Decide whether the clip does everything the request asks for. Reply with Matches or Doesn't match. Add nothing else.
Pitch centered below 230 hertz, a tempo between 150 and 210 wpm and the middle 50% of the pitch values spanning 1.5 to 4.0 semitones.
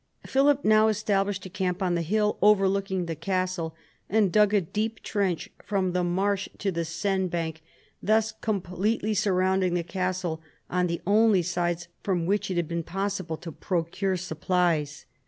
Matches